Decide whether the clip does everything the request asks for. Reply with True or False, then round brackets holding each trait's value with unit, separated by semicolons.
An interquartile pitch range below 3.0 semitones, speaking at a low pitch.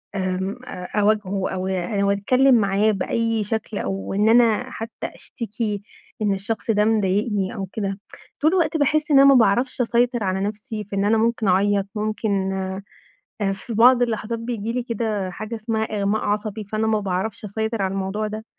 False (2.6 semitones; 215 Hz)